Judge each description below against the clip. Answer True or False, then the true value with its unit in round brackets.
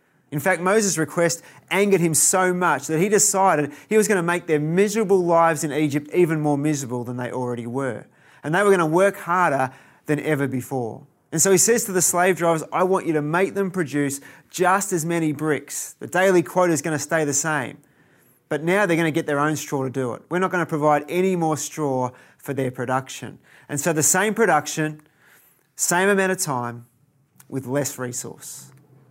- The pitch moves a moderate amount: True (4.3 semitones)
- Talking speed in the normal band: False (210 wpm)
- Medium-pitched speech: True (155 Hz)